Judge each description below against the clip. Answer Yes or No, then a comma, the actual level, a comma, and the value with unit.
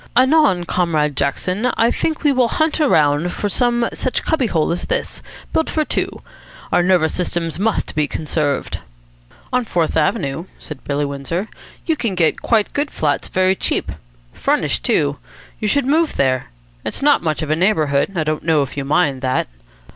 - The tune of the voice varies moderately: No, wide, 8.2 semitones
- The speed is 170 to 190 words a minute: Yes, average, 175 wpm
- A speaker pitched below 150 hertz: No, medium, 175 Hz